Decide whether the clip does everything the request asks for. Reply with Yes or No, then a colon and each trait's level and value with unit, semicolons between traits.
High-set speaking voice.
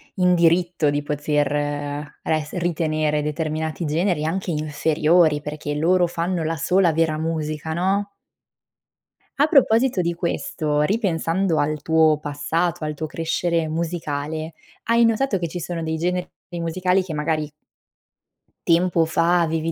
No: medium, 165 Hz